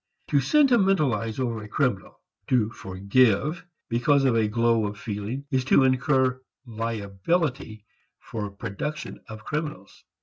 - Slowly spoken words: Yes, slow, 125 wpm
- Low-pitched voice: Yes, low, 120 Hz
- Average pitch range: Yes, average, 4.6 semitones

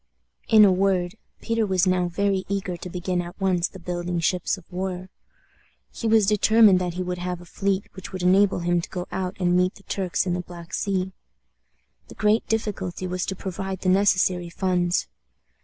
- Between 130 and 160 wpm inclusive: No, average, 190 wpm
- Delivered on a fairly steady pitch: Yes, narrow, 1.6 semitones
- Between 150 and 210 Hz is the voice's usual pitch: Yes, medium, 185 Hz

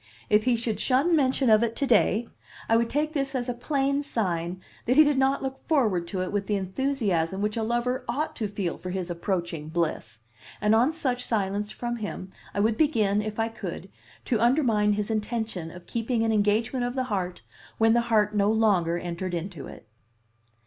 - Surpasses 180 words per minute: Yes, average, 200 wpm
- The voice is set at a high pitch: Yes, high, 220 Hz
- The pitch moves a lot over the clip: No, average, 4.5 semitones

